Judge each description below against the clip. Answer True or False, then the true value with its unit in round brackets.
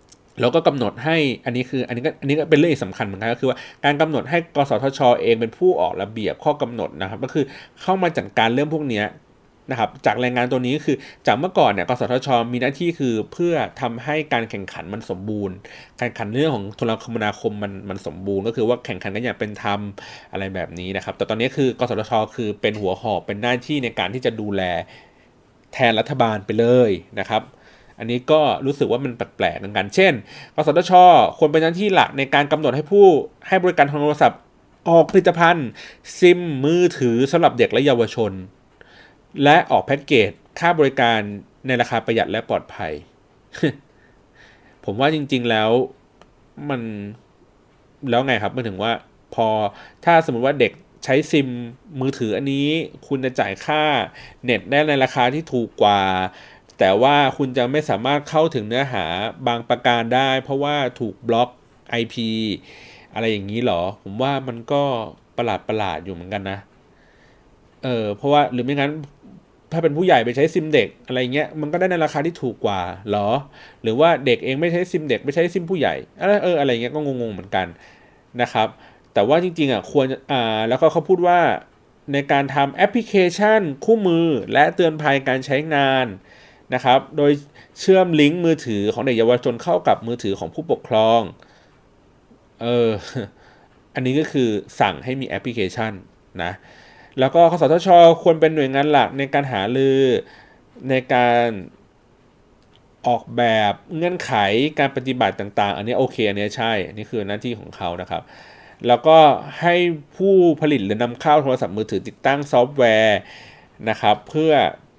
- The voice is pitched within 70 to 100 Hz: False (130 Hz)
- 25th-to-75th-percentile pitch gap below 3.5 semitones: False (5.3 semitones)